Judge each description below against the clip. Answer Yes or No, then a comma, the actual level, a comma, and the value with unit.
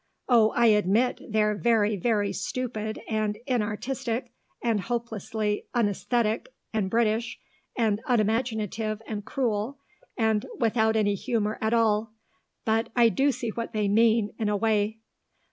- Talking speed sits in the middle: No, slow, 130 wpm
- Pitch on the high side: Yes, high, 220 Hz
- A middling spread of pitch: No, narrow, 1.9 semitones